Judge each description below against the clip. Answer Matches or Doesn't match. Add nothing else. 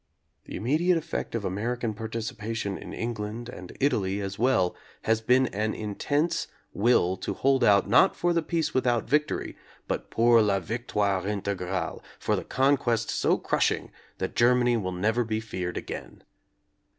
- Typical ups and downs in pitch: Matches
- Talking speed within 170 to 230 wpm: Doesn't match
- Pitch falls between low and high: Doesn't match